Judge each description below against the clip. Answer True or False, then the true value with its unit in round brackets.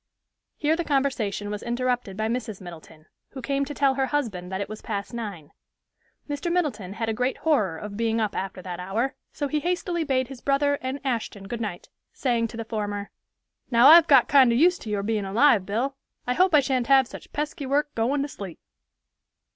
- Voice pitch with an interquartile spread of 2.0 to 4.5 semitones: False (5.2 semitones)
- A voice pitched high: True (240 Hz)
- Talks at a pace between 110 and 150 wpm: False (205 wpm)